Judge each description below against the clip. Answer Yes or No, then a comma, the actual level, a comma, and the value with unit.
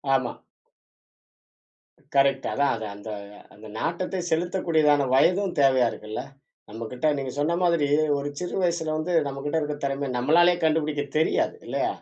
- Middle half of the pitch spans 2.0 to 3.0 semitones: No, average, 3.8 semitones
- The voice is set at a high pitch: No, medium, 150 Hz